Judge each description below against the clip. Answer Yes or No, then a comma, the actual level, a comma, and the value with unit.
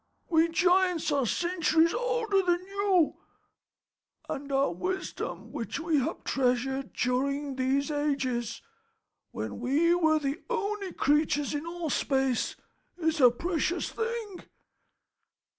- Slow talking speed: Yes, slow, 115 wpm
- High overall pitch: Yes, very high, 315 Hz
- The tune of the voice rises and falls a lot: No, average, 4.8 semitones